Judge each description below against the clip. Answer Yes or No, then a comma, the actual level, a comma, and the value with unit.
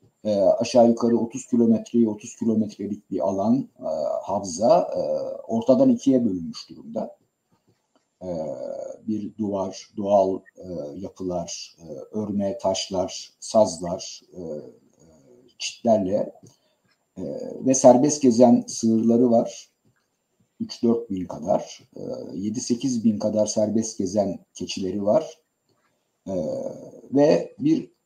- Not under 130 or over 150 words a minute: No, average, 105 wpm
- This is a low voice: Yes, low, 120 Hz